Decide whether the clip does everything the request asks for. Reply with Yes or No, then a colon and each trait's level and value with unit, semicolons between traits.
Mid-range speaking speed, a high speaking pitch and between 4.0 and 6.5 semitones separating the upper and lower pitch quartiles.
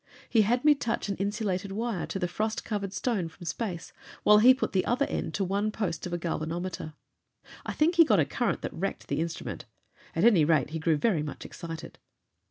No: fast, 210 wpm; high, 195 Hz; average, 5.0 semitones